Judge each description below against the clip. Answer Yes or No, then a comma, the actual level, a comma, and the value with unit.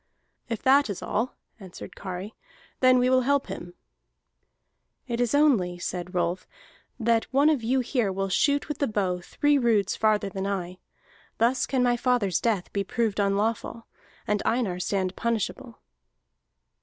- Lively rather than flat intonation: No, average, 4.7 semitones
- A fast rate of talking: No, average, 155 wpm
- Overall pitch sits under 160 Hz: No, high, 225 Hz